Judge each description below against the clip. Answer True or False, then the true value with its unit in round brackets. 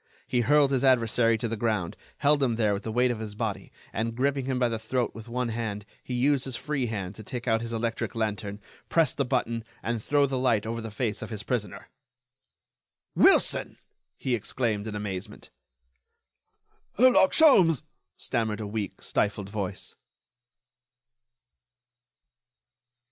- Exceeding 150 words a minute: True (160 wpm)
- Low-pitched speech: True (115 Hz)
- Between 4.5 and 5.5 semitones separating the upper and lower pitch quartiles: False (3.1 semitones)